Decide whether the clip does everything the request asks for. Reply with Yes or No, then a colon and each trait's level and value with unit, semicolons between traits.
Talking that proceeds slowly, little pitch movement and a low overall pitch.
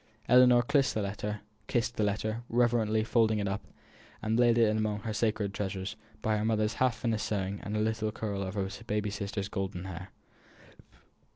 No: average, 165 wpm; narrow, 1.8 semitones; low, 110 Hz